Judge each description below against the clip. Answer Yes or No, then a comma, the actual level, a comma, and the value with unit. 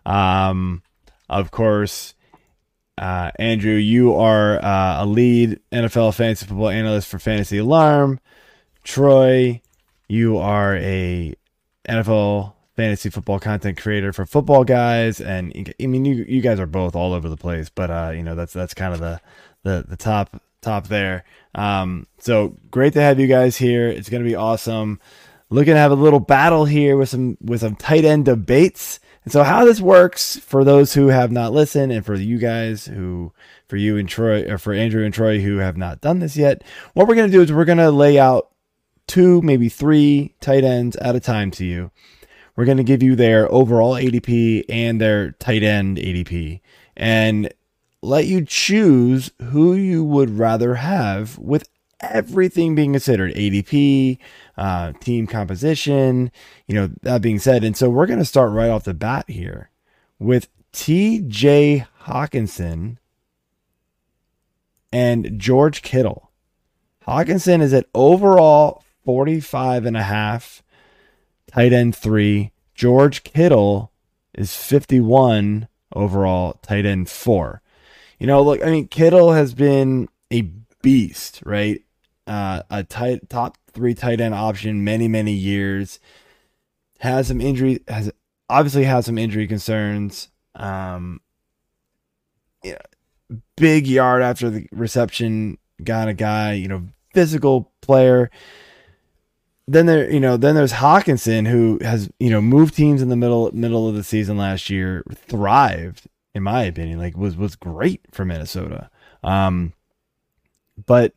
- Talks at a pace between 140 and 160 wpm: Yes, average, 150 wpm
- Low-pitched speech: Yes, low, 115 Hz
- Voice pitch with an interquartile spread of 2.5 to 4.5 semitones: No, average, 4.9 semitones